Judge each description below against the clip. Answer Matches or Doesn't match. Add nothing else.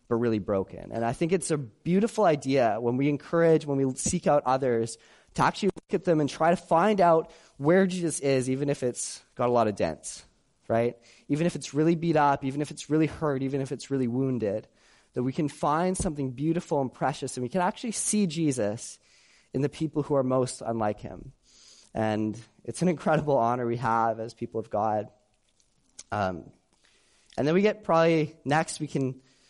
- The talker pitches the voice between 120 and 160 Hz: Matches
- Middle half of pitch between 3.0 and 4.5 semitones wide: Doesn't match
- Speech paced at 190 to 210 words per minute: Matches